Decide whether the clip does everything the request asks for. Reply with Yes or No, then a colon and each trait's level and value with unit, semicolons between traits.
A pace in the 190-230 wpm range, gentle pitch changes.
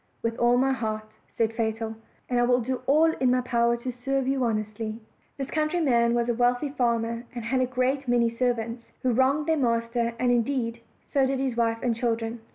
Yes: average, 200 wpm; narrow, 2.1 semitones